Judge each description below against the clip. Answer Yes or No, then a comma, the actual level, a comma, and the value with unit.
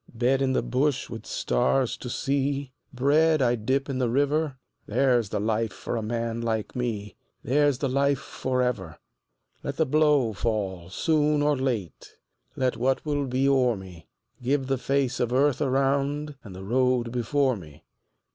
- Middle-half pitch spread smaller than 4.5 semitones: Yes, average, 3.3 semitones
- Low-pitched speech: Yes, low, 130 Hz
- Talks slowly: No, average, 165 wpm